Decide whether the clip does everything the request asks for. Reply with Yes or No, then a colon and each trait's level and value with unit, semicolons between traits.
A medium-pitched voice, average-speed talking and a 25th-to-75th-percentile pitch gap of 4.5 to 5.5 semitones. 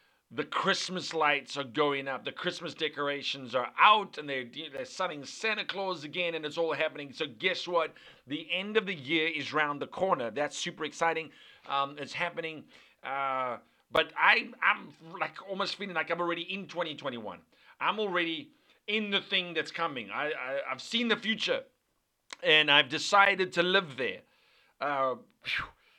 Yes: medium, 165 Hz; average, 165 wpm; average, 4.9 semitones